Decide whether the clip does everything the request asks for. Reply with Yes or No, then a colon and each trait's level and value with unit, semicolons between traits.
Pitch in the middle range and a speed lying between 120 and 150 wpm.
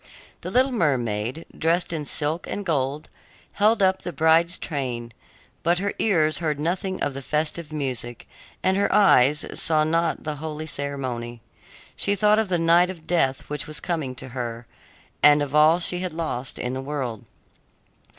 No: medium, 155 Hz; average, 170 wpm